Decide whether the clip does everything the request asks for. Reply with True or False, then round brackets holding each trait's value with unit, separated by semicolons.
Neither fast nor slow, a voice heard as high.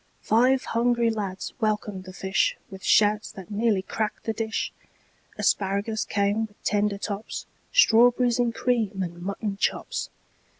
False (120 wpm; 210 Hz)